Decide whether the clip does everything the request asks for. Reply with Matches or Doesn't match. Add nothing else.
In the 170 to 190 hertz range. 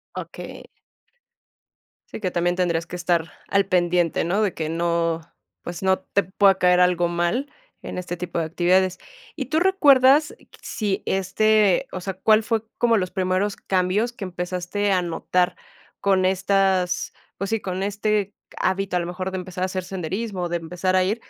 Matches